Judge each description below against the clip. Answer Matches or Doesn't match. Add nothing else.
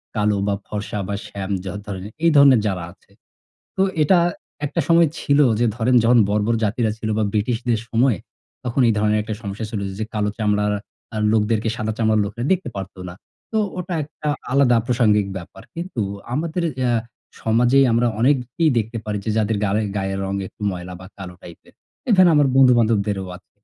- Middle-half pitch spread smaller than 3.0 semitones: Doesn't match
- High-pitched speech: Doesn't match